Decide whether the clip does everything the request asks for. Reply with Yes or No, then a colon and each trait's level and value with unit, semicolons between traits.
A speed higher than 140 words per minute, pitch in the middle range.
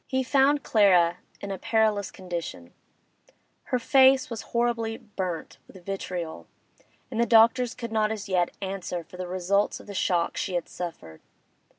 No: average, 160 wpm; high, 200 Hz